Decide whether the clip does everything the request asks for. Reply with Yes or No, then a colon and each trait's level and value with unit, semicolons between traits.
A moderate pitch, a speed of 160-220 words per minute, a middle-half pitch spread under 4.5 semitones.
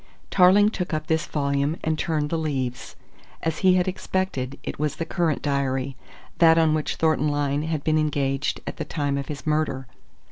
Yes: medium, 155 Hz; average, 185 wpm; narrow, 2.6 semitones